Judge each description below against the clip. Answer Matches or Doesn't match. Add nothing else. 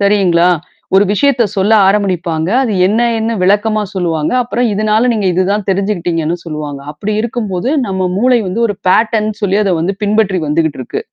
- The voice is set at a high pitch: Matches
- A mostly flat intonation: Doesn't match